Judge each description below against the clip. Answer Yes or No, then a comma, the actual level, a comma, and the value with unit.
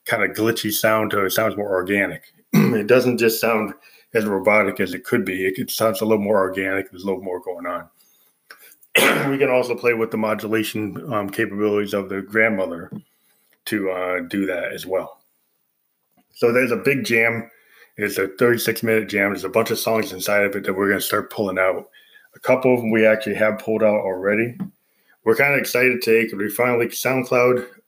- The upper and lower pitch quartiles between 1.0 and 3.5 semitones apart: Yes, average, 2.8 semitones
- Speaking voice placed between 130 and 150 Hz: No, low, 110 Hz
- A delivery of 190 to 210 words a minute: Yes, average, 200 wpm